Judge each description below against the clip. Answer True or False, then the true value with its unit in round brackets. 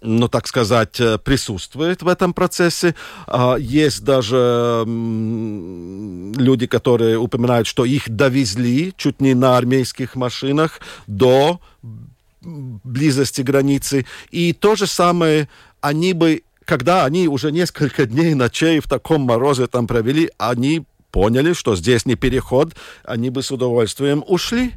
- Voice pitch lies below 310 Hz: True (135 Hz)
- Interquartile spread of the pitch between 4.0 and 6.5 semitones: True (4.3 semitones)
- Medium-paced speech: True (125 wpm)